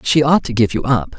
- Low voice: Yes, low, 125 Hz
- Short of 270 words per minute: No, fast, 305 wpm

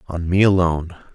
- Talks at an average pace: Yes, average, 155 wpm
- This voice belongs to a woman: No, male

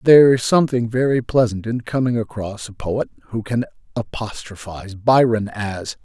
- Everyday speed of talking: Yes, average, 150 wpm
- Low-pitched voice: Yes, low, 115 Hz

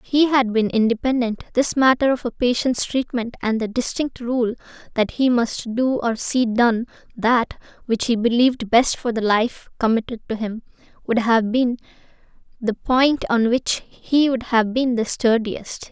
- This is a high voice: Yes, high, 235 Hz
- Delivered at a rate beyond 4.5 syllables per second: No, 4.4 syllables/s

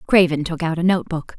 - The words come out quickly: Yes, fast, 260 wpm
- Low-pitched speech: No, medium, 170 Hz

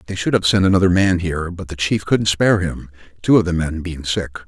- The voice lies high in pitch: No, very low, 90 Hz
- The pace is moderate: No, fast, 255 wpm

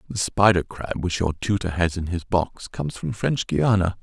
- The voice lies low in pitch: Yes, very low, 90 Hz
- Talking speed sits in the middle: No, fast, 210 wpm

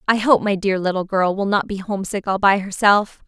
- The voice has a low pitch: No, high, 195 Hz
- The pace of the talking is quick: Yes, fast, 240 wpm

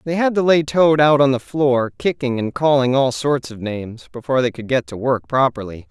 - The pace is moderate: No, fast, 235 wpm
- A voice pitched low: Yes, low, 130 Hz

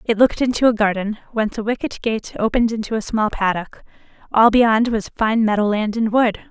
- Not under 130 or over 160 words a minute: No, fast, 205 wpm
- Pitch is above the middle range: Yes, high, 220 Hz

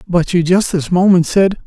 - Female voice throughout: No, male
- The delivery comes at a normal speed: No, fast, 215 wpm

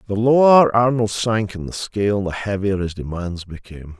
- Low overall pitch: Yes, low, 105 Hz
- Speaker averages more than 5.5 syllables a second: No, 5.0 syllables/s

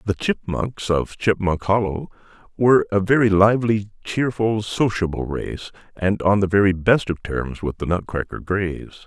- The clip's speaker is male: Yes, male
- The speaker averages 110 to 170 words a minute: Yes, average, 150 wpm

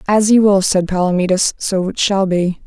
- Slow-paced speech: No, average, 200 wpm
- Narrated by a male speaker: No, female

